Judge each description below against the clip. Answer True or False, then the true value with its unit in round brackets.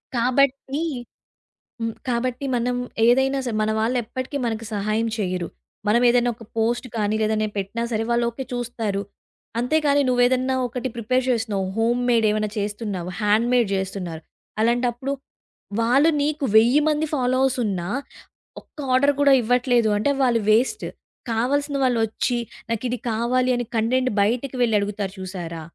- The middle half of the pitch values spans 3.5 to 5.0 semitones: False (2.9 semitones)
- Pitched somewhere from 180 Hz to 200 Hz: False (235 Hz)